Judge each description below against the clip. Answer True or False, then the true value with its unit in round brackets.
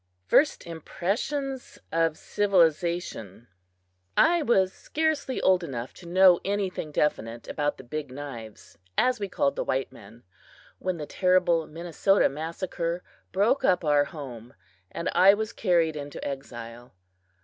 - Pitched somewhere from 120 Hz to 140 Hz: False (170 Hz)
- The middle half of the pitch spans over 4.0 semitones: True (5.2 semitones)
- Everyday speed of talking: False (130 wpm)